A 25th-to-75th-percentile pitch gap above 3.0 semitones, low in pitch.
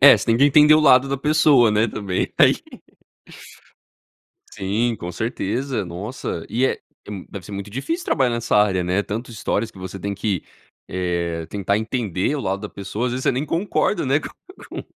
Yes: average, 5.1 semitones; low, 110 Hz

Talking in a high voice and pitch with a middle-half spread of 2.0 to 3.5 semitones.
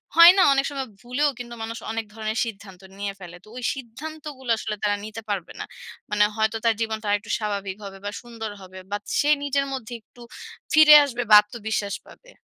No: high, 225 Hz; average, 4.2 semitones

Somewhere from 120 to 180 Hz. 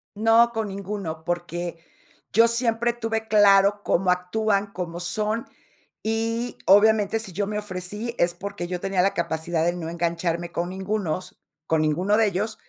No: high, 195 Hz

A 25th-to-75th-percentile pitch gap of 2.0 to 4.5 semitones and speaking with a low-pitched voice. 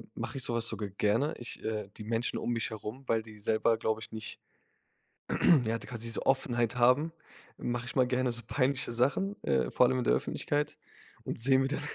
Yes: average, 2.9 semitones; low, 120 Hz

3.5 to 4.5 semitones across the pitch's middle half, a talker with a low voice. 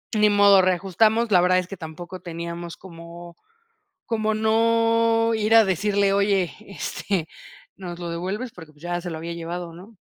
No: average, 3.8 semitones; medium, 185 Hz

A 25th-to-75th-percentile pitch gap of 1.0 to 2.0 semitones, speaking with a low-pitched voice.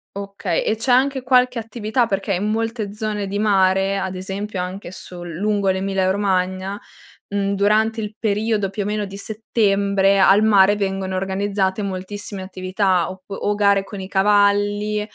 No: narrow, 1.7 semitones; high, 200 Hz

